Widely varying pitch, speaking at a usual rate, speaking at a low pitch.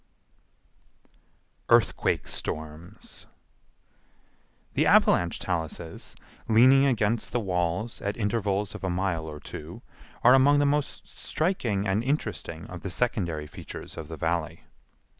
No: wide, 6.1 semitones; slow, 120 wpm; very low, 95 Hz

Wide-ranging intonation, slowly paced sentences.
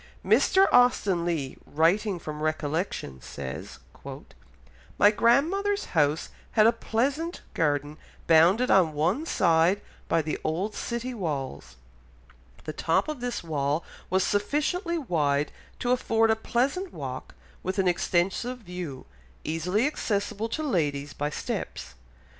Yes: wide, 7.5 semitones; slow, 125 wpm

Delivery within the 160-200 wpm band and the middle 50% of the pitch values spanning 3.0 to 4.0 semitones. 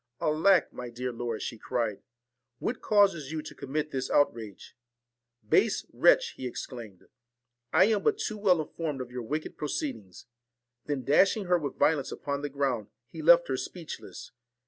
No: average, 190 wpm; average, 4.9 semitones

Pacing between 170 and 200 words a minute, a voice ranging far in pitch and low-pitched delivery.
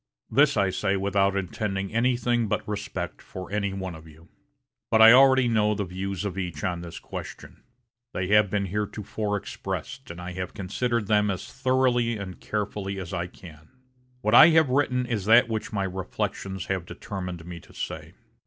No: average, 180 wpm; average, 3.5 semitones; low, 100 Hz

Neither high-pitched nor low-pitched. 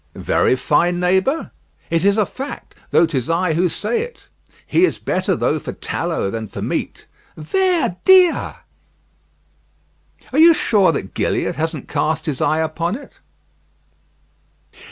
Yes: medium, 175 Hz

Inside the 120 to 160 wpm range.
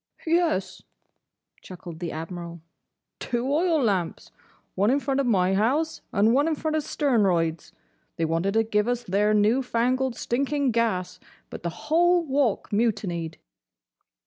Yes: average, 145 wpm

